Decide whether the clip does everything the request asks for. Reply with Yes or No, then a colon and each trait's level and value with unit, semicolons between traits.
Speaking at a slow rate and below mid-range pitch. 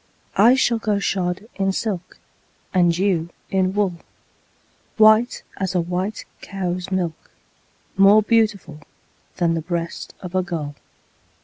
No: slow, 125 wpm; medium, 185 Hz